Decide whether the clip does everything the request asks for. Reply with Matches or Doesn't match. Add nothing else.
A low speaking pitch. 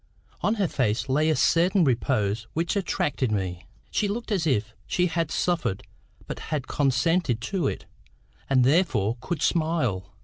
Doesn't match